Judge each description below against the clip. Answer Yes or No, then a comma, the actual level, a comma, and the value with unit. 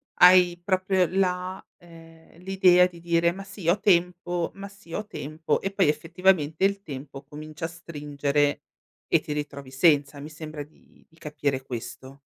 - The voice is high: No, medium, 165 Hz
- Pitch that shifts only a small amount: No, average, 3.7 semitones